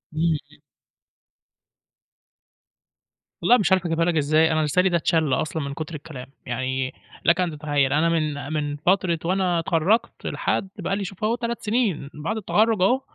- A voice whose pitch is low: No, medium, 165 Hz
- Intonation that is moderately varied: Yes, average, 4.3 semitones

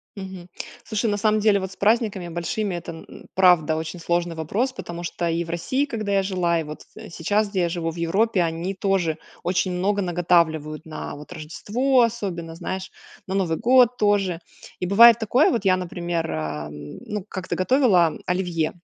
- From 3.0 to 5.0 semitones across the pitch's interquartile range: Yes, average, 3.6 semitones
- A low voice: No, medium, 185 Hz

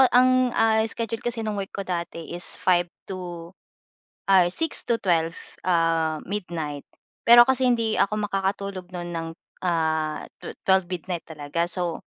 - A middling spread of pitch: Yes, average, 4.1 semitones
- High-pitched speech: No, medium, 180 Hz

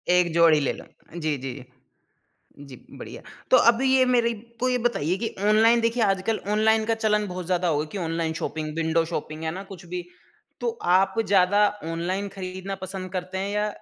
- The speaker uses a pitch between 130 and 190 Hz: Yes, medium, 185 Hz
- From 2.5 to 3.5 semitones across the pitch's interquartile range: No, average, 4.5 semitones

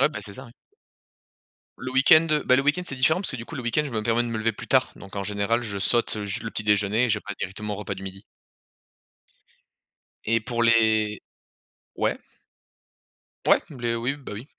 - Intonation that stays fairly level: No, average, 3.5 semitones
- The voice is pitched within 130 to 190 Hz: No, low, 115 Hz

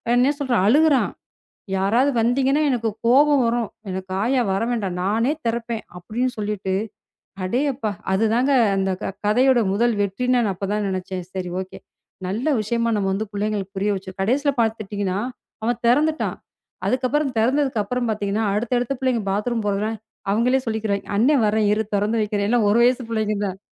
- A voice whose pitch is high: Yes, high, 220 Hz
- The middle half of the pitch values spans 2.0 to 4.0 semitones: Yes, average, 3.6 semitones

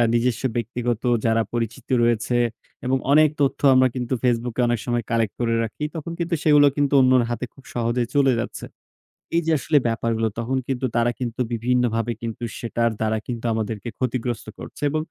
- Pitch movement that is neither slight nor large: No, narrow, 2.0 semitones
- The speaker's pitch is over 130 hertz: No, low, 120 Hz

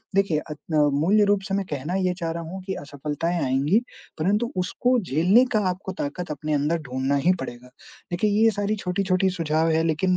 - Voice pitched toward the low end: No, medium, 170 Hz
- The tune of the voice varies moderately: Yes, average, 4.3 semitones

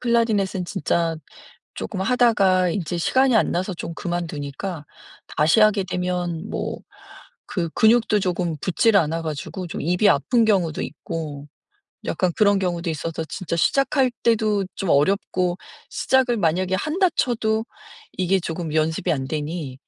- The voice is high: No, medium, 180 Hz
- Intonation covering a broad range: No, average, 4.4 semitones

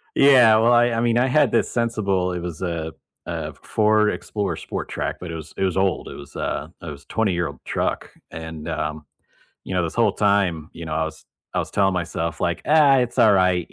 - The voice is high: No, very low, 95 Hz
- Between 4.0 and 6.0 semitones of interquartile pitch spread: Yes, wide, 5.4 semitones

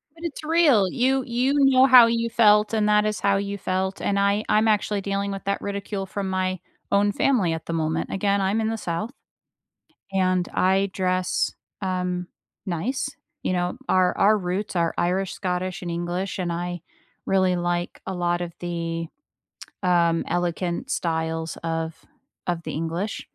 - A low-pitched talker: No, high, 190 Hz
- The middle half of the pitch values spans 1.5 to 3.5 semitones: Yes, average, 3.1 semitones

